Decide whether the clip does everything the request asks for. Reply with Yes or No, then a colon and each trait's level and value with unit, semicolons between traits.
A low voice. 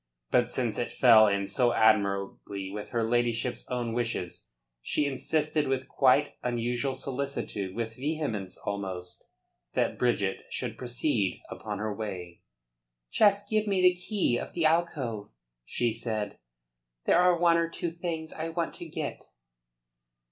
Yes: low, 120 Hz